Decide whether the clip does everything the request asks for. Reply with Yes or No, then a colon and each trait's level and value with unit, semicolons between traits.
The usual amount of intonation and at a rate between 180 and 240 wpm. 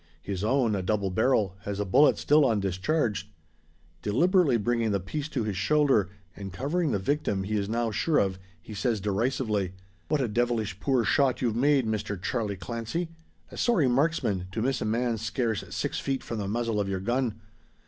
Yes: average, 4.8 semitones; average, 185 wpm